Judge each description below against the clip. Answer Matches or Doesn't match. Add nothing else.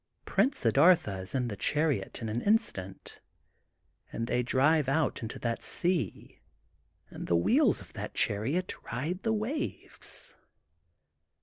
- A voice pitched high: Doesn't match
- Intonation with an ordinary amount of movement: Doesn't match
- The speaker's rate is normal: Doesn't match